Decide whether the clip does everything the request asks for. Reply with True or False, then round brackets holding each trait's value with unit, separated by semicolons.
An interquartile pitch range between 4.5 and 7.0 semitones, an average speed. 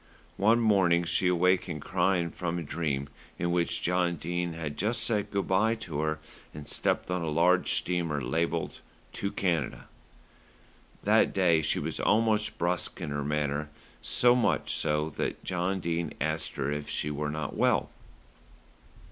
False (3.2 semitones; 160 wpm)